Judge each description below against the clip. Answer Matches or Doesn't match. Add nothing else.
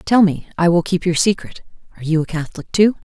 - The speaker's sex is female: Matches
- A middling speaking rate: Matches